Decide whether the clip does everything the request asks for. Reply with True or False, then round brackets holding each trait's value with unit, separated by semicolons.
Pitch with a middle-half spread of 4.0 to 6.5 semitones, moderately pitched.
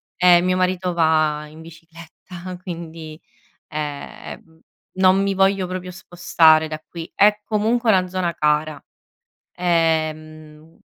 False (2.8 semitones; 170 Hz)